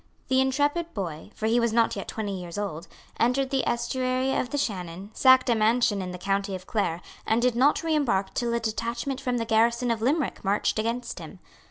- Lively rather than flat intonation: No, average, 4.2 semitones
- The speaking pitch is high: Yes, high, 235 Hz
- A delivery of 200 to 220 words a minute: Yes, fast, 205 wpm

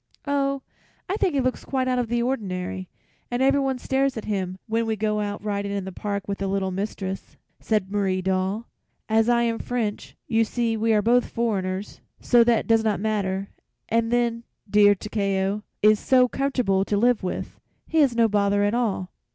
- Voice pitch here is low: No, high, 215 Hz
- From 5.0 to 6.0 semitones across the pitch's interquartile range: No, average, 3.3 semitones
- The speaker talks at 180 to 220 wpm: Yes, average, 190 wpm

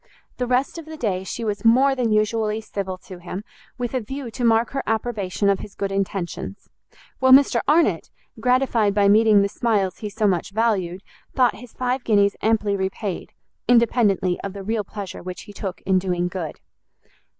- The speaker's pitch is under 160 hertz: No, high, 210 Hz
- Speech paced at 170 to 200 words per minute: Yes, average, 185 wpm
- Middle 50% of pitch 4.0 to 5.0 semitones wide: No, average, 3.5 semitones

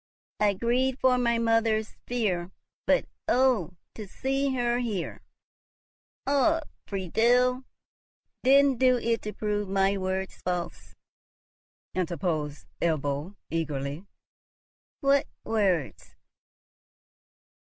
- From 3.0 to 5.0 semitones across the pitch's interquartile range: No, wide, 5.6 semitones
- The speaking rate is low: Yes, slow, 90 wpm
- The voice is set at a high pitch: Yes, high, 215 Hz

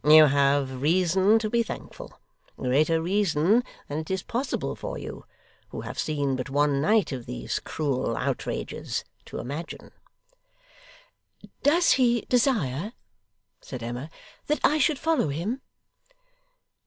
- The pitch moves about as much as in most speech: No, wide, 8.3 semitones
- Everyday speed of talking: No, slow, 130 wpm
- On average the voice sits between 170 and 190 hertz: No, medium, 160 Hz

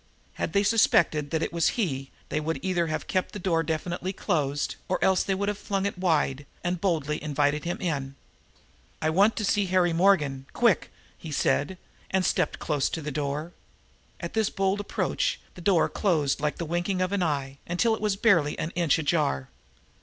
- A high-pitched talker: No, medium, 170 Hz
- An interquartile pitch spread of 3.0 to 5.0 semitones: Yes, average, 4.2 semitones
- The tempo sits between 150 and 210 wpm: Yes, average, 195 wpm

